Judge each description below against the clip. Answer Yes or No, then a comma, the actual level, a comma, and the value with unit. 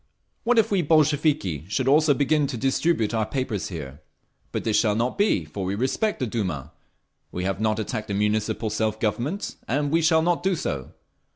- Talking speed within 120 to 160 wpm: No, average, 190 wpm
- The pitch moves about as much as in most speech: No, wide, 6.7 semitones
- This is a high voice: No, low, 115 Hz